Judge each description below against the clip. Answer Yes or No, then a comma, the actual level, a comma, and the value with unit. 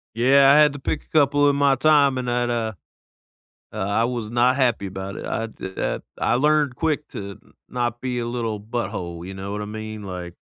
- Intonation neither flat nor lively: Yes, average, 5.0 semitones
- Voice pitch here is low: Yes, low, 120 Hz